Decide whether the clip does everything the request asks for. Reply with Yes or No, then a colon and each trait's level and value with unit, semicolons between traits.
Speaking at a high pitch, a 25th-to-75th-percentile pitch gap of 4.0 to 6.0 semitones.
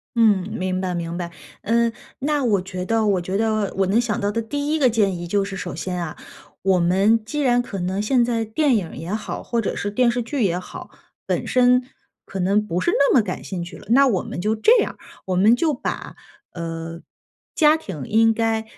Yes: high, 210 Hz; average, 4.5 semitones